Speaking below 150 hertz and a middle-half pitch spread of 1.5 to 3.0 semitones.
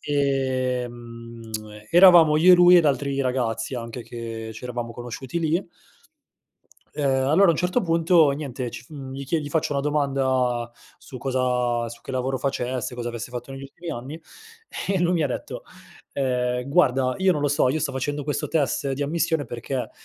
No: low, 135 Hz; average, 3.6 semitones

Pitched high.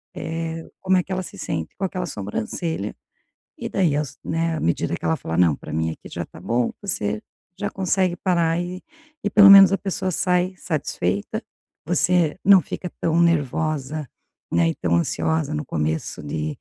No: medium, 160 Hz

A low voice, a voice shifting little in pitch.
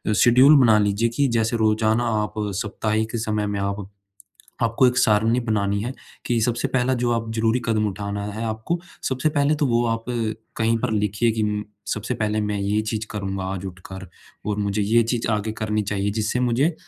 Yes: low, 110 Hz; narrow, 2.2 semitones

